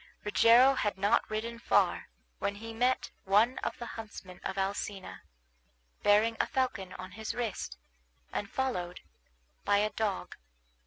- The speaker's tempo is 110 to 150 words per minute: Yes, average, 140 wpm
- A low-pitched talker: No, high, 215 Hz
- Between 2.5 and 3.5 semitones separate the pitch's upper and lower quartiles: Yes, average, 2.9 semitones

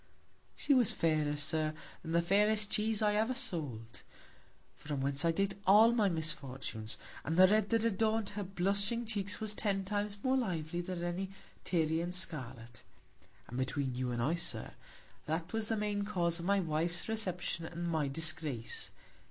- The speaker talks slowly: No, average, 165 wpm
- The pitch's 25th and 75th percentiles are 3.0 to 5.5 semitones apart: Yes, average, 5.1 semitones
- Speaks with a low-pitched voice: No, medium, 175 Hz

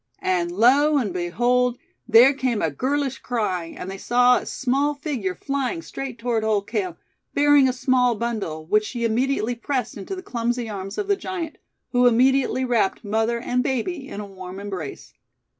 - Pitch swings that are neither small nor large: Yes, average, 4.5 semitones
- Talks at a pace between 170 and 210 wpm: Yes, average, 175 wpm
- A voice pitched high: Yes, high, 240 Hz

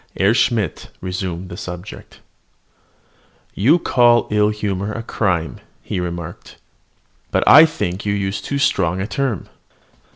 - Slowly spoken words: Yes, slow, 130 wpm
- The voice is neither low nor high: No, low, 100 Hz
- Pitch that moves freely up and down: No, average, 4.1 semitones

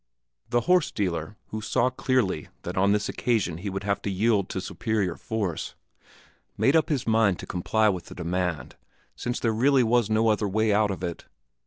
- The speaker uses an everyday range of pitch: Yes, average, 3.5 semitones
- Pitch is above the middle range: No, low, 105 Hz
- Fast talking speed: No, average, 190 wpm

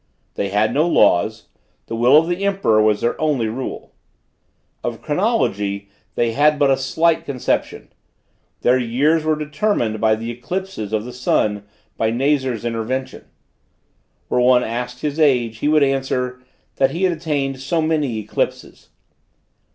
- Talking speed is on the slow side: No, average, 150 wpm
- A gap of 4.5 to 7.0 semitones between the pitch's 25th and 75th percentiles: Yes, average, 5.0 semitones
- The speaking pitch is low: Yes, low, 130 Hz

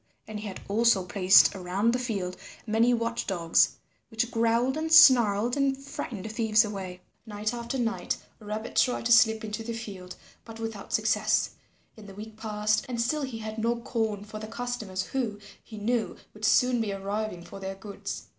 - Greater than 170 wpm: Yes, average, 180 wpm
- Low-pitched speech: No, high, 220 Hz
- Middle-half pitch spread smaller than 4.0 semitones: Yes, narrow, 2.4 semitones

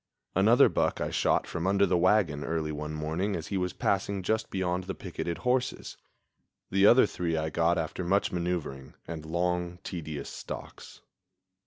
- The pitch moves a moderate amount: Yes, average, 3.3 semitones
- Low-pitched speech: Yes, very low, 90 Hz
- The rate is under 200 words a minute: Yes, average, 165 wpm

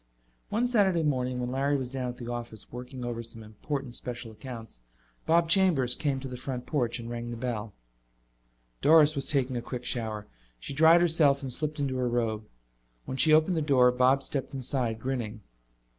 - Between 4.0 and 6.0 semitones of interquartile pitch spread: No, average, 3.3 semitones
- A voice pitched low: Yes, low, 130 Hz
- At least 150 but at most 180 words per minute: No, average, 190 wpm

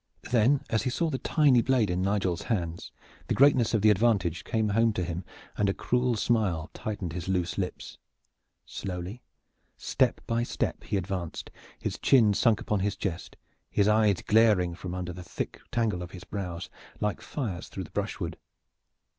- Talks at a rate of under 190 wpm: Yes, average, 170 wpm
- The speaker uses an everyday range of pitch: Yes, average, 4.4 semitones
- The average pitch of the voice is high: No, low, 100 Hz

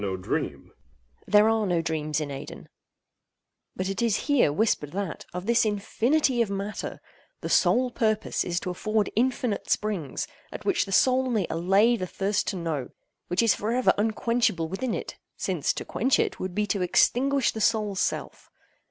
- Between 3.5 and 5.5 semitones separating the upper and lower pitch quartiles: Yes, average, 4.5 semitones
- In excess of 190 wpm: No, average, 160 wpm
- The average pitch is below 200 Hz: No, high, 210 Hz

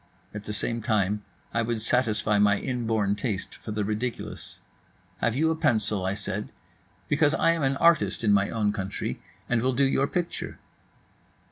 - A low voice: Yes, low, 110 Hz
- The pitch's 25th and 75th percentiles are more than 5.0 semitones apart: No, average, 3.9 semitones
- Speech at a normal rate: Yes, average, 170 wpm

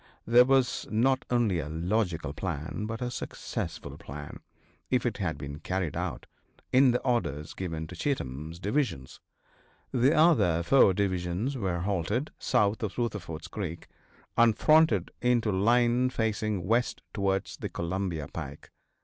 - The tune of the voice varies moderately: No, wide, 6.1 semitones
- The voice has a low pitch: Yes, low, 100 Hz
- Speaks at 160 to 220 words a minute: No, average, 140 wpm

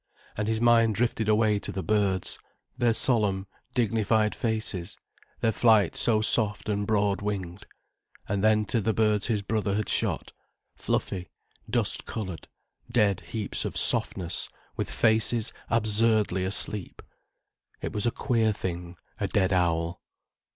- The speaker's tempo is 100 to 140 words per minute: Yes, slow, 135 wpm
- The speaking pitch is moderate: No, low, 105 Hz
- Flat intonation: Yes, narrow, 2.2 semitones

